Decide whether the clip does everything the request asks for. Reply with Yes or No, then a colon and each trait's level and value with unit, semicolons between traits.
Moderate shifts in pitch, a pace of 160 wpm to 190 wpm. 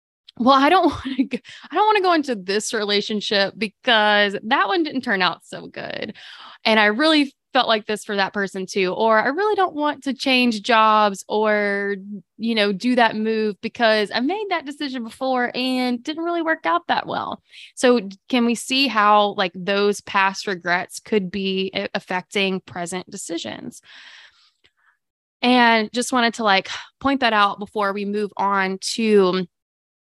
Yes: average, 4.1 semitones; average, 170 wpm